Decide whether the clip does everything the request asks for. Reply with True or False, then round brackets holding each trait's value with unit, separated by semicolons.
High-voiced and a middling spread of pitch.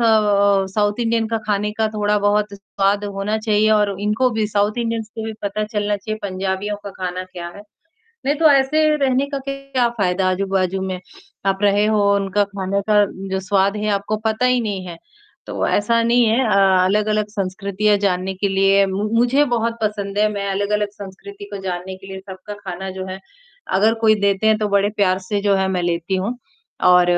False (205 Hz; 2.0 semitones)